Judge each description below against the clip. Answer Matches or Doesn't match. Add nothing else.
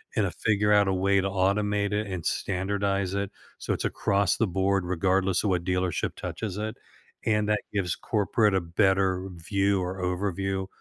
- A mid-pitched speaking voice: Doesn't match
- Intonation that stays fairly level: Matches